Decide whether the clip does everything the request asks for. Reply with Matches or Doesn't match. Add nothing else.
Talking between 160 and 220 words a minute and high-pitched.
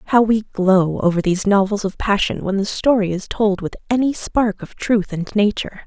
Matches